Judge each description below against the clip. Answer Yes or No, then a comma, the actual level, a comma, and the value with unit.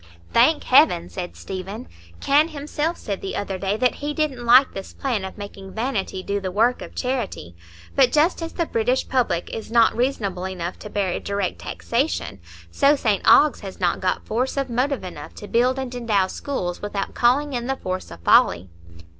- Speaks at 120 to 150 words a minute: No, average, 190 wpm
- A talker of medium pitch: No, high, 225 Hz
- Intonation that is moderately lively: No, wide, 5.7 semitones